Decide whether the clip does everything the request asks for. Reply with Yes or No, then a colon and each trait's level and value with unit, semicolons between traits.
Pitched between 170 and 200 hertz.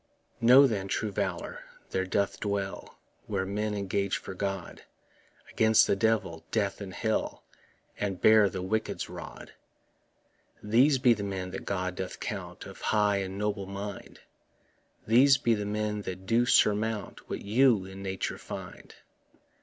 No: low, 100 Hz